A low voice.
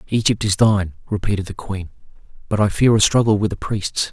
Yes: low, 105 Hz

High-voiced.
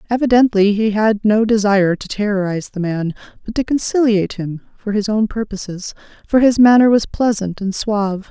Yes: high, 210 Hz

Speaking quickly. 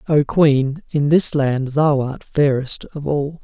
No: average, 175 wpm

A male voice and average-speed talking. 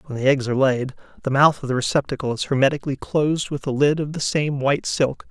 No: male; fast, 235 wpm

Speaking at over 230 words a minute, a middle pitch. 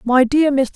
No: fast, 240 wpm; very high, 265 Hz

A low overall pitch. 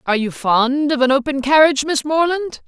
No: very high, 280 Hz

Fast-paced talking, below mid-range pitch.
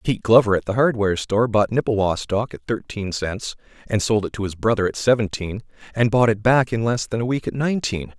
Yes: fast, 225 wpm; low, 110 Hz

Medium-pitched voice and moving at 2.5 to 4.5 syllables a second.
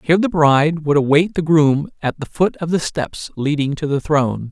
No: medium, 155 Hz; 5.2 syllables/s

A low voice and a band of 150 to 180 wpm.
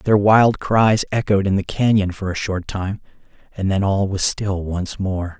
No: low, 100 Hz; average, 200 wpm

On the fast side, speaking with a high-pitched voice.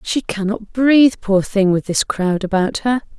No: average, 190 wpm; high, 210 Hz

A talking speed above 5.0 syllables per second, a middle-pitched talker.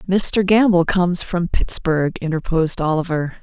No: 4.8 syllables/s; medium, 175 Hz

